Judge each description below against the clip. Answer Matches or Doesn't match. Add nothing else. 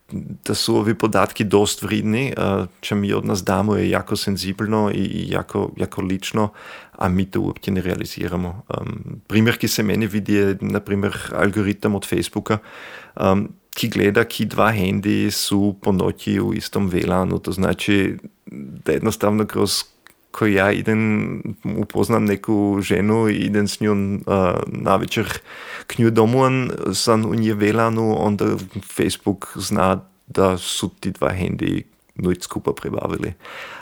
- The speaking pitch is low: Matches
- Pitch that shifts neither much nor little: Doesn't match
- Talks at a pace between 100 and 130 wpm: Doesn't match